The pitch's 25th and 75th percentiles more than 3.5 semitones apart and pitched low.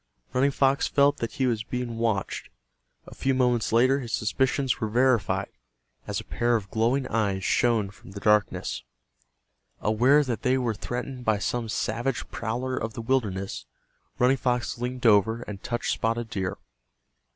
No: average, 2.8 semitones; low, 120 Hz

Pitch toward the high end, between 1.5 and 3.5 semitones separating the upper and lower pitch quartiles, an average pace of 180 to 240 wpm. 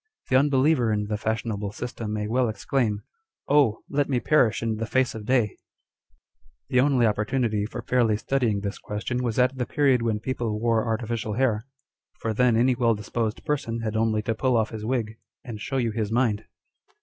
No: low, 115 Hz; average, 2.8 semitones; average, 190 wpm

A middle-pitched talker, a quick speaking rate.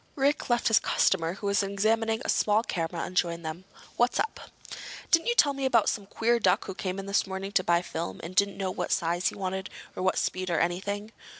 No: high, 195 Hz; fast, 225 wpm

